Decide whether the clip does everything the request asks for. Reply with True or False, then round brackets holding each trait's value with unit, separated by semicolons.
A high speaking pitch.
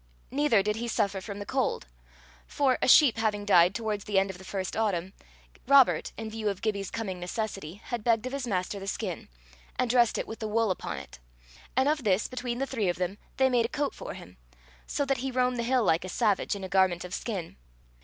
True (215 Hz)